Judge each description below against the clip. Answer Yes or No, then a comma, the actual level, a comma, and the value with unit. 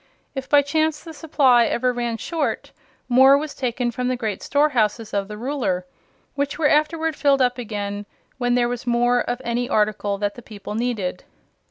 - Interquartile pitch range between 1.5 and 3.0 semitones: No, average, 4.4 semitones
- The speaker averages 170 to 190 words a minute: Yes, average, 180 wpm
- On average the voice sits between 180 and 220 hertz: No, high, 245 Hz